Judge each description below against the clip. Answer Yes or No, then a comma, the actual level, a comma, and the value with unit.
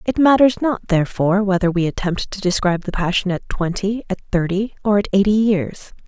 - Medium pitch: No, high, 195 Hz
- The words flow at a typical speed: Yes, average, 190 wpm